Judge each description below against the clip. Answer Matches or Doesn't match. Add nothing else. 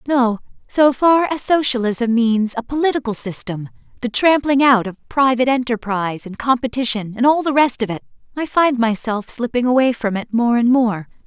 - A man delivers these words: Doesn't match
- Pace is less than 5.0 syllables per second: Doesn't match